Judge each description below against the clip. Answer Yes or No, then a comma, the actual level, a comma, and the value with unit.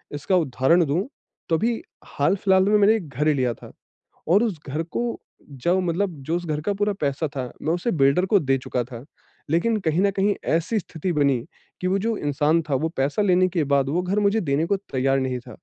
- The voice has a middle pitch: Yes, medium, 165 Hz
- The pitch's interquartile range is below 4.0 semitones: No, wide, 5.6 semitones